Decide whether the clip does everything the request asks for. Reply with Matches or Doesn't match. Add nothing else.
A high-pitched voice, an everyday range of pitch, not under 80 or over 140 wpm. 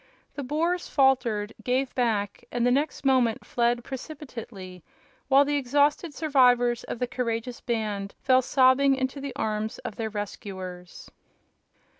Matches